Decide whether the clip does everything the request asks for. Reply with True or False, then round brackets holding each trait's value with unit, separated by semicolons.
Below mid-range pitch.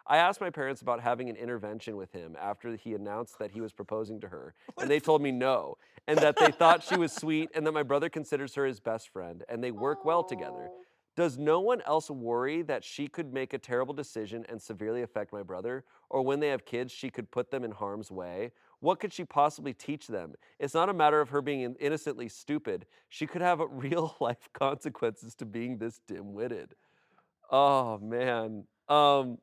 True (130 Hz)